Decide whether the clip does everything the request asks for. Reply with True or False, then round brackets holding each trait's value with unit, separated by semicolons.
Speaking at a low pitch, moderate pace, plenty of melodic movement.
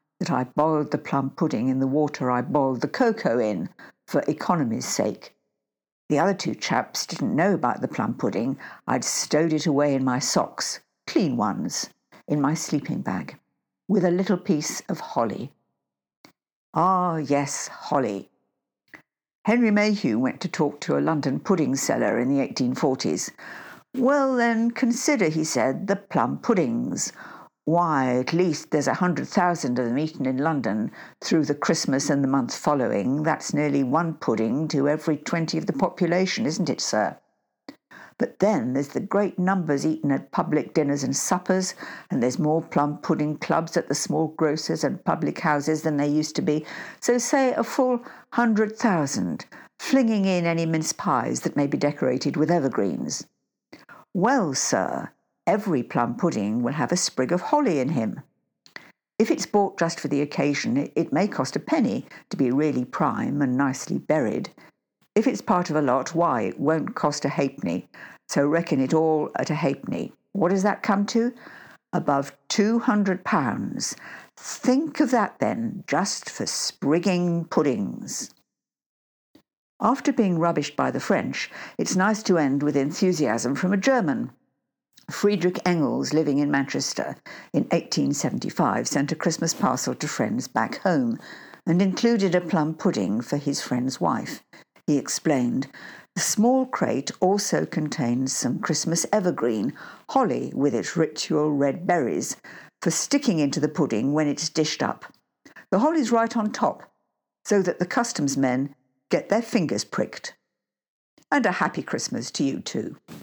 False (165 Hz; 160 wpm; 6.1 semitones)